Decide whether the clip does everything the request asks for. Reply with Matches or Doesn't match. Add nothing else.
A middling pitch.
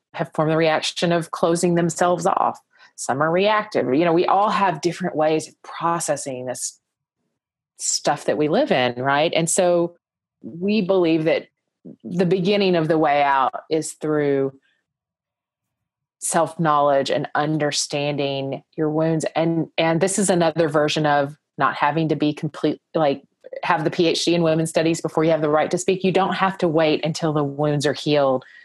Matches